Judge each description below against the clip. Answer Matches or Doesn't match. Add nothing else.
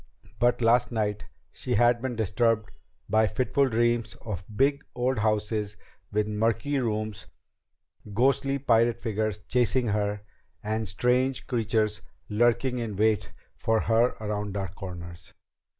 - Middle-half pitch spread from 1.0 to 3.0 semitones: Matches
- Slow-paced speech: Matches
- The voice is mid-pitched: Doesn't match